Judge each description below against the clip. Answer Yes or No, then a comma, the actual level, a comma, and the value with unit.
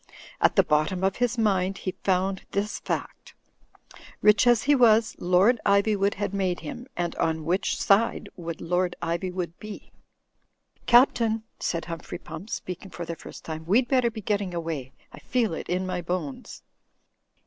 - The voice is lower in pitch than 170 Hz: No, high, 190 Hz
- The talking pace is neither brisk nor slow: Yes, average, 165 wpm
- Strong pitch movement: No, average, 3.8 semitones